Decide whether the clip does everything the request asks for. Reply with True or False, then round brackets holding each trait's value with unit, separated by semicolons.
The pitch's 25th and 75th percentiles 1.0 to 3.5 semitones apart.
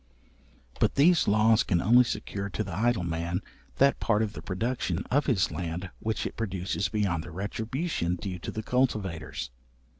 False (4.6 semitones)